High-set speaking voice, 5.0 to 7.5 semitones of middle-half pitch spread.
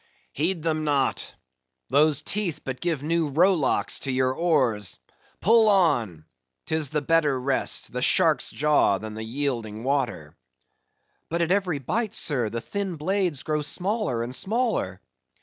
No: medium, 150 Hz; wide, 5.4 semitones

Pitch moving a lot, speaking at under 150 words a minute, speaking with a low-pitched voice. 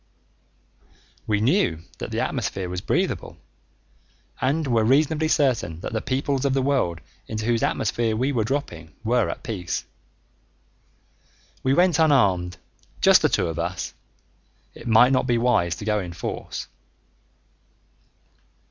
Yes: wide, 6.5 semitones; average, 140 wpm; low, 115 Hz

